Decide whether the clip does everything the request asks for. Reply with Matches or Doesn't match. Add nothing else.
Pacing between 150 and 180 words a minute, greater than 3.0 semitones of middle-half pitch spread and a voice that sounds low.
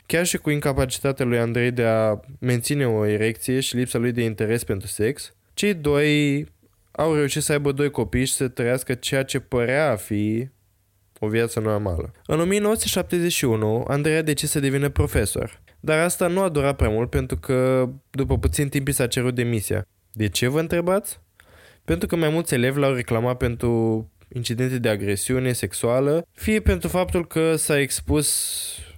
Matches